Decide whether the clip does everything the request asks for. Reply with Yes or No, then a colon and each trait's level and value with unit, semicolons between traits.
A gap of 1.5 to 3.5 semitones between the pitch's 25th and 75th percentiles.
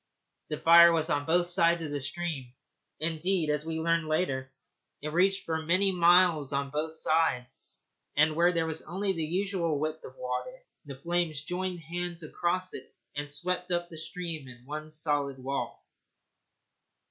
Yes: average, 3.0 semitones